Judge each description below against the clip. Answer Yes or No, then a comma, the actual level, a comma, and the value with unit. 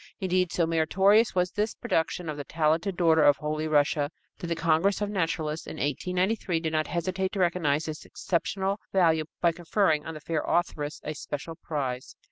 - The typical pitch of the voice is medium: Yes, medium, 165 Hz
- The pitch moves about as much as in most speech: Yes, average, 3.1 semitones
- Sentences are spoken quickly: No, average, 180 wpm